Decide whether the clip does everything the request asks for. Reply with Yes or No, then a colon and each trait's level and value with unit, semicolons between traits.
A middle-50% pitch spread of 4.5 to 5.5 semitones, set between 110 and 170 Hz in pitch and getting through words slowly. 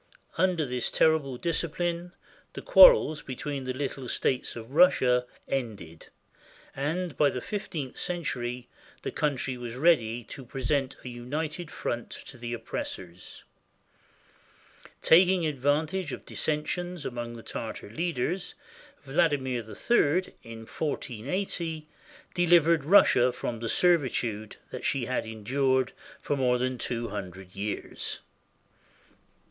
Yes: average, 5.2 semitones; low, 135 Hz; slow, 120 wpm